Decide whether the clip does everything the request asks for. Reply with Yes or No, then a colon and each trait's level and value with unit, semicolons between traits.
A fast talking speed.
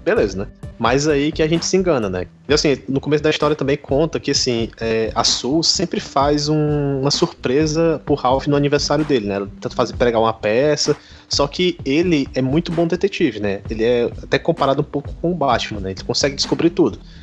Yes: fast, 215 wpm